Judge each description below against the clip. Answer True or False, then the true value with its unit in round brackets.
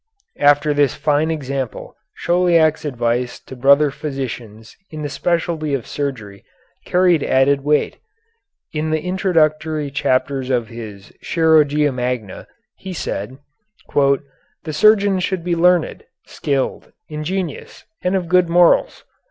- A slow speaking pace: True (120 wpm)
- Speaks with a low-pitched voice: False (150 Hz)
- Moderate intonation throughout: True (3.8 semitones)